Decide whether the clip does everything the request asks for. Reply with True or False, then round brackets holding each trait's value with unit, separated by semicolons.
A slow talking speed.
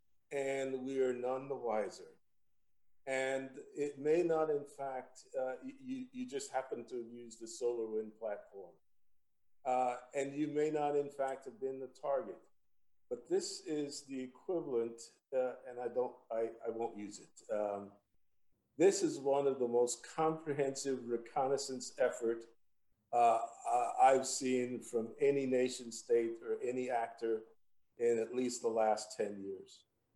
False (150 wpm)